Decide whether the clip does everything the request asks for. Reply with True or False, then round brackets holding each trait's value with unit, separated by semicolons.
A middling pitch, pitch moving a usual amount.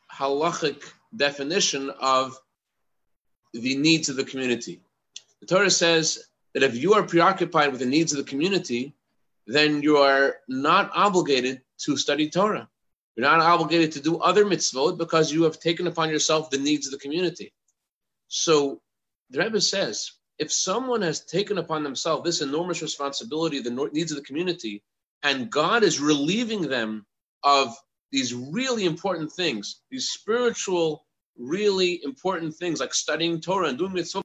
True (160 Hz; 4.3 semitones)